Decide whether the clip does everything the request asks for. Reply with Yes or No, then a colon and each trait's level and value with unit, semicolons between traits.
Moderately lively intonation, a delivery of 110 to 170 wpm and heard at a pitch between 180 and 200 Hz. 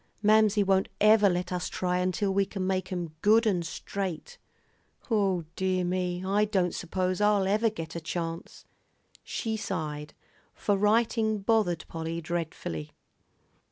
Yes: average, 3.0 semitones; average, 140 wpm; high, 190 Hz